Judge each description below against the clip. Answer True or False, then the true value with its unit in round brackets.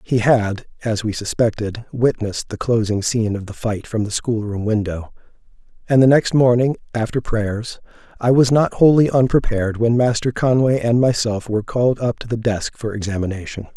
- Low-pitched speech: True (115 Hz)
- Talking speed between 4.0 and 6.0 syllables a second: True (5.2 syllables/s)